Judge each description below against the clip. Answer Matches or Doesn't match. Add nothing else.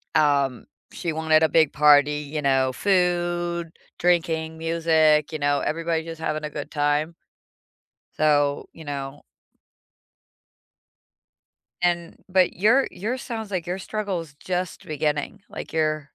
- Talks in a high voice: Doesn't match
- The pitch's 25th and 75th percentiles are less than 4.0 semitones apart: Matches